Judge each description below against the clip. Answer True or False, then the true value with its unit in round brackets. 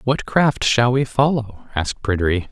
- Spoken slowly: False (165 wpm)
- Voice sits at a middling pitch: False (115 Hz)